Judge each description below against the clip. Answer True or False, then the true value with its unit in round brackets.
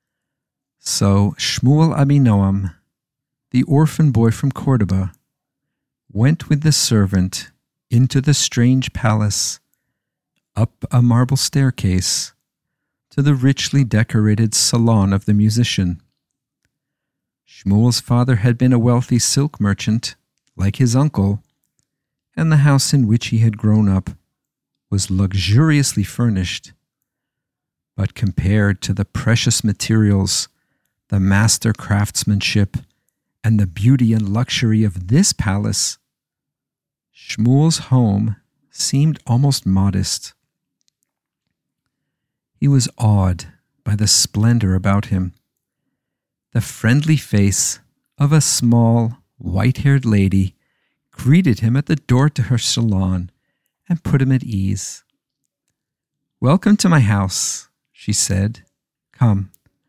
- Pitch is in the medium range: False (120 Hz)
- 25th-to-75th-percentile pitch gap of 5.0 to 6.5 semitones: True (5.3 semitones)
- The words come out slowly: True (110 wpm)